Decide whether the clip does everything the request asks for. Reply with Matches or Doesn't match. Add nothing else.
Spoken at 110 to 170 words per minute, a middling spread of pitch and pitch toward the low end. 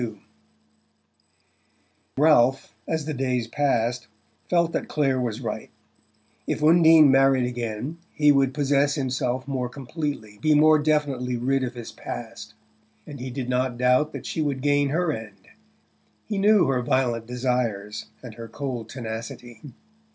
Matches